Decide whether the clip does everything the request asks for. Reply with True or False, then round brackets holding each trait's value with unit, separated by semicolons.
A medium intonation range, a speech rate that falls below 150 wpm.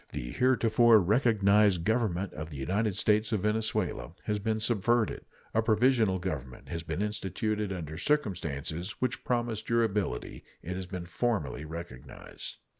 True (4.4 semitones; 135 wpm)